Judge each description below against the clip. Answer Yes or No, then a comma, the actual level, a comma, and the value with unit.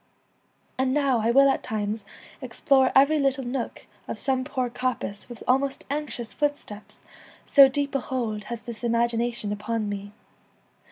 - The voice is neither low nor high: No, very high, 250 Hz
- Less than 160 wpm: Yes, average, 150 wpm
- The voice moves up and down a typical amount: Yes, average, 3.3 semitones